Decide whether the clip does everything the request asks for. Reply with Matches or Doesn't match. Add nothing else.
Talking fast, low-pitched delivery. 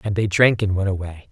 Matches